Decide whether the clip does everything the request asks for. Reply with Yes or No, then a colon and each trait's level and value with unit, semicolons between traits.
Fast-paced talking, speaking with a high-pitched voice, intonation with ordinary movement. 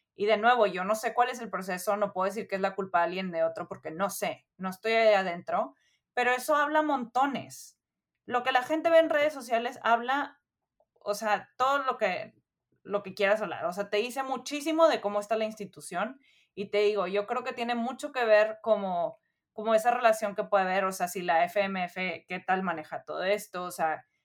Yes: fast, 220 wpm; high, 210 Hz; average, 4.6 semitones